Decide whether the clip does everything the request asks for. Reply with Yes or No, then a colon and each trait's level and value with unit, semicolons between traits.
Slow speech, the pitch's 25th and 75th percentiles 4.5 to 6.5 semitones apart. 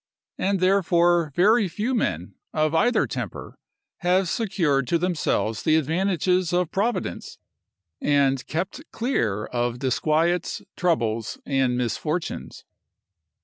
Yes: slow, 105 wpm; wide, 5.6 semitones